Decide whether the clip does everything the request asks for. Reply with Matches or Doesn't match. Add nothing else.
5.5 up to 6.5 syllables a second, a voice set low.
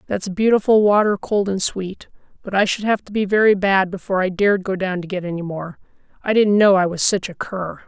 Doesn't match